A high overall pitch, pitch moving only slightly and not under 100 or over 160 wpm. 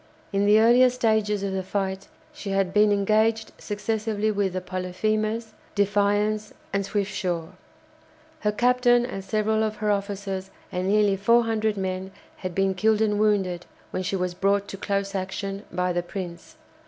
Yes: high, 200 Hz; narrow, 2.1 semitones; average, 155 wpm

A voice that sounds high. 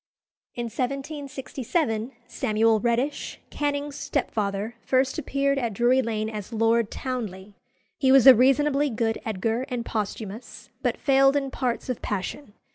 Yes: high, 245 Hz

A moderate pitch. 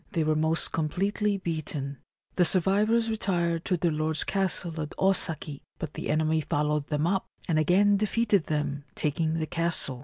Yes: medium, 165 Hz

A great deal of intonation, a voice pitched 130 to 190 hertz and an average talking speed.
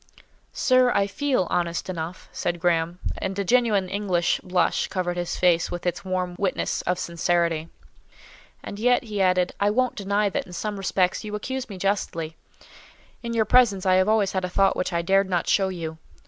No: average, 2.7 semitones; medium, 185 Hz; average, 190 wpm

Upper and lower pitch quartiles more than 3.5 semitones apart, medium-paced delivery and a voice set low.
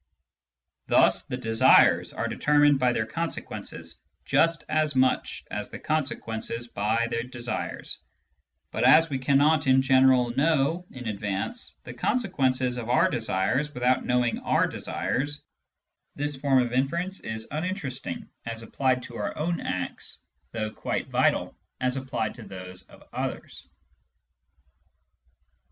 No: average, 4.0 semitones; slow, 130 wpm; low, 130 Hz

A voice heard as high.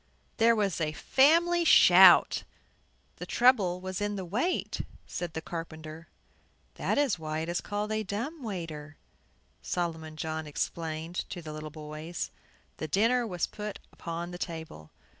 No: medium, 175 Hz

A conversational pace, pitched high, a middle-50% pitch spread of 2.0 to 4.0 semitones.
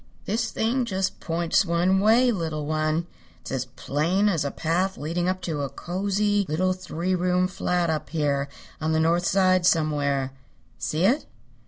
No: average, 170 wpm; medium, 175 Hz; average, 3.4 semitones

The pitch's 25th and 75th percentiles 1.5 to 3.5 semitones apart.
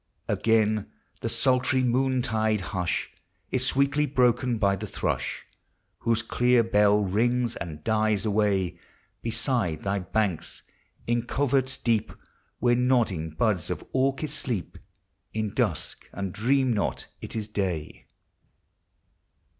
No: average, 3.9 semitones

